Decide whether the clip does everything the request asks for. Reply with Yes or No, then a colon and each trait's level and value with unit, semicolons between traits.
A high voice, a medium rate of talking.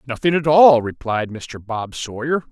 No: low, 130 Hz; average, 165 wpm